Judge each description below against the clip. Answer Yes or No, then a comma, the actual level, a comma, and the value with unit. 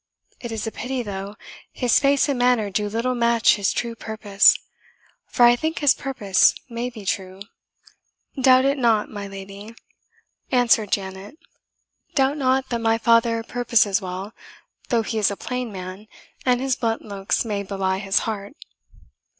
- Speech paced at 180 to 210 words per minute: No, average, 160 wpm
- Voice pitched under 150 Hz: No, high, 225 Hz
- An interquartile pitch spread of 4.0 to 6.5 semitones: No, average, 3.6 semitones